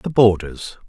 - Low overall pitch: Yes, low, 105 Hz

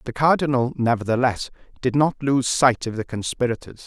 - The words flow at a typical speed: Yes, average, 155 wpm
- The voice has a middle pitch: No, low, 125 Hz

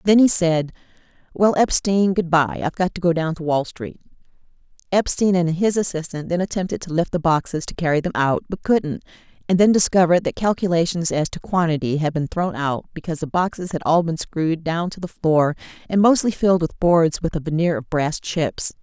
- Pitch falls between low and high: Yes, medium, 170 Hz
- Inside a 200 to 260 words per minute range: Yes, fast, 205 wpm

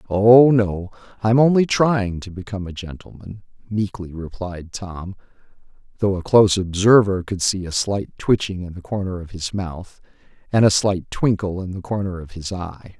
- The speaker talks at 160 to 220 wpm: Yes, average, 170 wpm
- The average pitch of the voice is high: No, low, 100 Hz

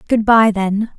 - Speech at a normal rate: Yes, average, 185 wpm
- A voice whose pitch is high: Yes, high, 215 Hz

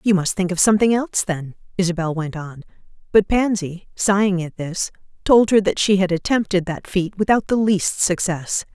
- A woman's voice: Yes, female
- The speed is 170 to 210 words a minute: Yes, average, 185 wpm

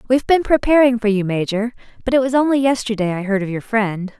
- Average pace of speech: No, fast, 230 wpm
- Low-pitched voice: No, high, 230 Hz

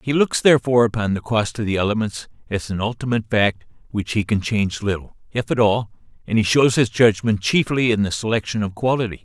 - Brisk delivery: Yes, fast, 210 wpm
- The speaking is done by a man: Yes, male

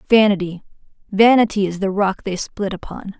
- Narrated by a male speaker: No, female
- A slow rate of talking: Yes, slow, 130 wpm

